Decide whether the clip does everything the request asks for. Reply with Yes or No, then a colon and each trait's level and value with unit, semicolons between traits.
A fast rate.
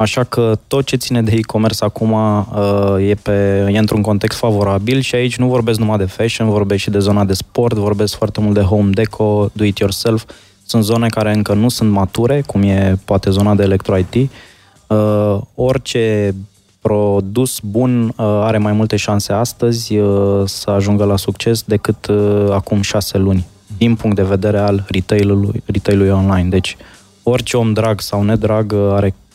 Yes: fast, 175 wpm